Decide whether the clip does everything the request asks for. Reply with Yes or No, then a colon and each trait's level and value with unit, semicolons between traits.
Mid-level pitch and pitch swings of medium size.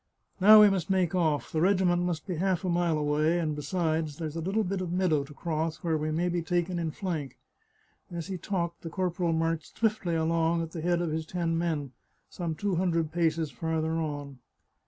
No: medium, 165 Hz; narrow, 2.0 semitones